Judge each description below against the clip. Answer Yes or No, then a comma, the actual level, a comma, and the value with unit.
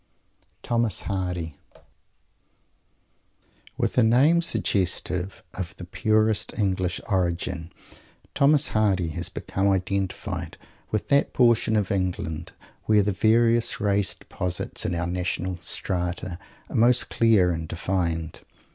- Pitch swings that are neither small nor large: Yes, average, 3.7 semitones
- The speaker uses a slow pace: Yes, slow, 110 wpm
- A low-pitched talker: Yes, very low, 95 Hz